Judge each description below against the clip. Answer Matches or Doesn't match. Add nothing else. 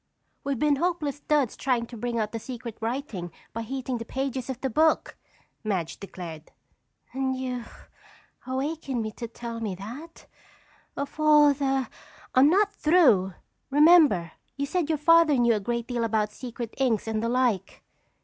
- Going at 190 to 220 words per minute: Doesn't match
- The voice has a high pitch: Matches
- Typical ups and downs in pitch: Matches